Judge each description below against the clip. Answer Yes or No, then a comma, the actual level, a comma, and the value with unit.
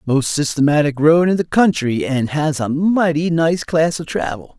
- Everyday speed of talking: Yes, average, 185 wpm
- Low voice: No, medium, 155 Hz